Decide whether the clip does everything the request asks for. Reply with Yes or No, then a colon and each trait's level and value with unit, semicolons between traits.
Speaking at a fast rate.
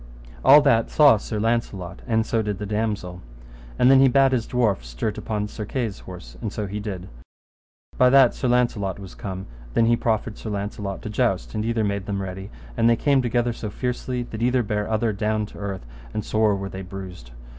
Yes: fast, 210 wpm